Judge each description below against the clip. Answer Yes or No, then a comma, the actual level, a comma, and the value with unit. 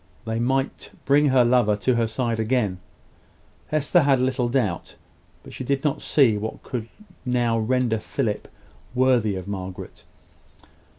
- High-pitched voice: No, low, 120 Hz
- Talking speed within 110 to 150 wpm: Yes, average, 140 wpm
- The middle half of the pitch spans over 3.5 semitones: No, average, 3.0 semitones